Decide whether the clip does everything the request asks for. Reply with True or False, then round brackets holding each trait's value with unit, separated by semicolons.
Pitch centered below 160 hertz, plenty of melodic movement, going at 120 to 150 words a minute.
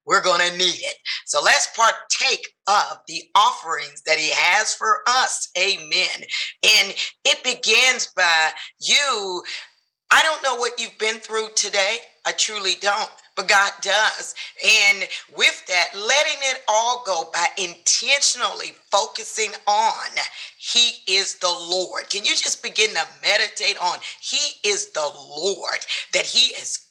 False (230 Hz; 7.4 semitones; 145 wpm)